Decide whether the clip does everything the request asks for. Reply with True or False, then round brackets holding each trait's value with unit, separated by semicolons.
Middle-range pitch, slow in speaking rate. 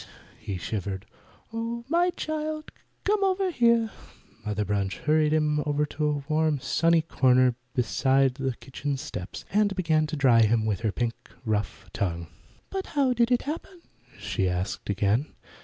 False (145 Hz; 155 wpm)